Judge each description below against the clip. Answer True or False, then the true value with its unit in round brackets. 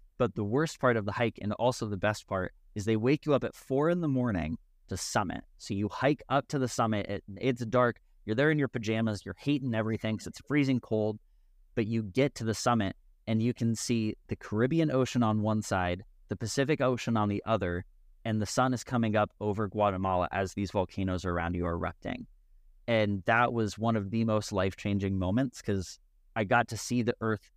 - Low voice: True (110 Hz)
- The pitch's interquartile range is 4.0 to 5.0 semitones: False (3.4 semitones)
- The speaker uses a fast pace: True (220 wpm)